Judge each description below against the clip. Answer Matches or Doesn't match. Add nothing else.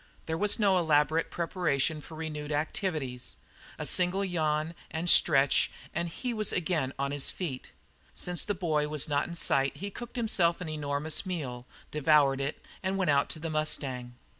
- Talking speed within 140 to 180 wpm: Matches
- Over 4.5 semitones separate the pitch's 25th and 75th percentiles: Doesn't match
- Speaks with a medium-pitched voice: Matches